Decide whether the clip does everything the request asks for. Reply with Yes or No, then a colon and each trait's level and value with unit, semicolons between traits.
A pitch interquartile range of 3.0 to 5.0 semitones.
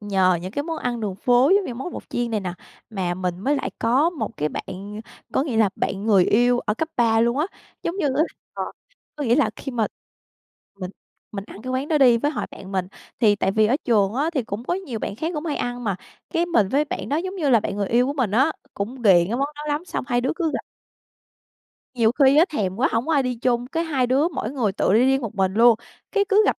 No: wide, 5.6 semitones